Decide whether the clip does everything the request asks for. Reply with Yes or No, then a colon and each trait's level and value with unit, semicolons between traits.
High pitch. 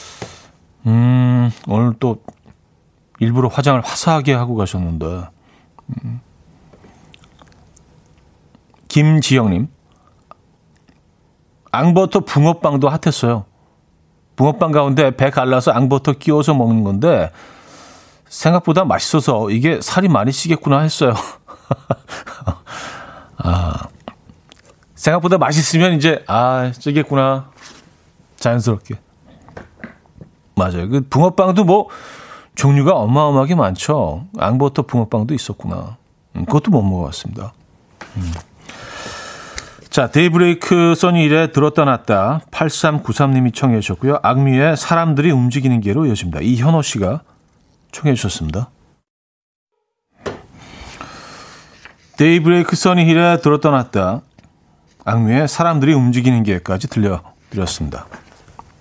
No: low, 135 Hz